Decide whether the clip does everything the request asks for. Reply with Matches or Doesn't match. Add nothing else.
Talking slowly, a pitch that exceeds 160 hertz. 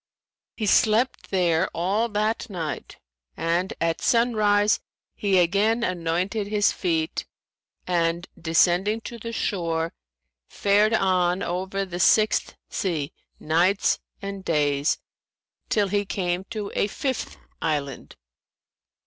Matches